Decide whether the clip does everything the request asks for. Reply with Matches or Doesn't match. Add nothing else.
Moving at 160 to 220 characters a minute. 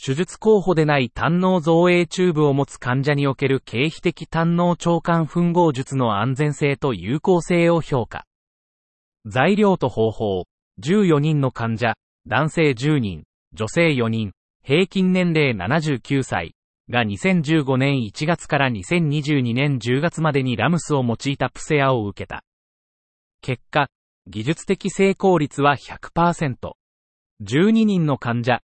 Matches